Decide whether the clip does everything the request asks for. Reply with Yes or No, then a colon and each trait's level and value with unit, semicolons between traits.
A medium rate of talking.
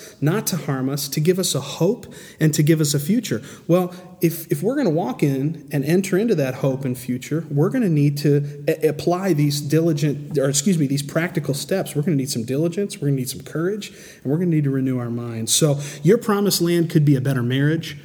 No: fast, 250 wpm